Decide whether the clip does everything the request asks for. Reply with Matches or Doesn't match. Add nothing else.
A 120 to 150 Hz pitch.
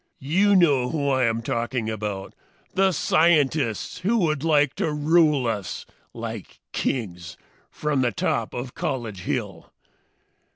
Matches